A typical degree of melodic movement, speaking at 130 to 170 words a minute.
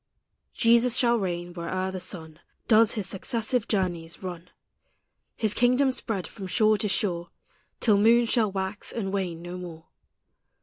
Yes: average, 4.2 semitones; average, 145 wpm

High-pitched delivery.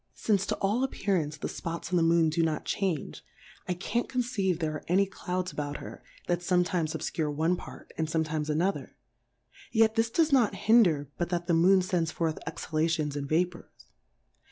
No: medium, 175 Hz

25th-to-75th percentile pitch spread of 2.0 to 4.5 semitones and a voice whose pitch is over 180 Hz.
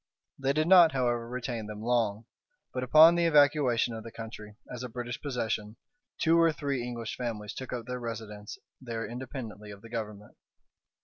No: average, 3.1 semitones; low, 120 Hz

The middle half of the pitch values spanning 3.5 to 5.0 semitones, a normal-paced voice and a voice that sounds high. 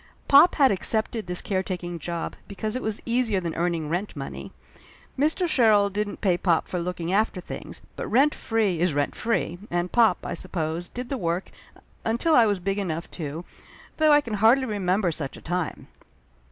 Yes: average, 4.6 semitones; average, 180 wpm; high, 195 Hz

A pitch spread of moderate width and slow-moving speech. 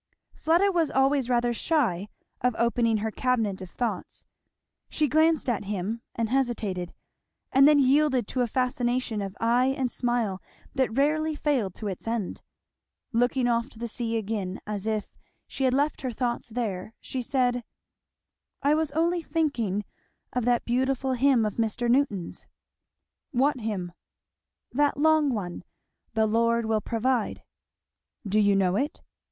No: average, 3.8 semitones; average, 150 wpm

